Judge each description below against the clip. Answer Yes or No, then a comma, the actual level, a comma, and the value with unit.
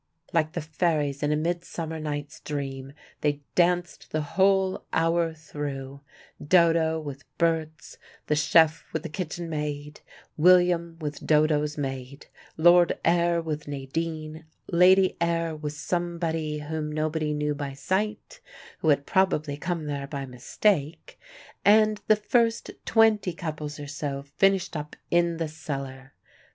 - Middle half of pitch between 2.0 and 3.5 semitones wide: Yes, average, 2.8 semitones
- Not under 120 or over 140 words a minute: Yes, slow, 135 wpm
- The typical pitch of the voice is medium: Yes, medium, 155 Hz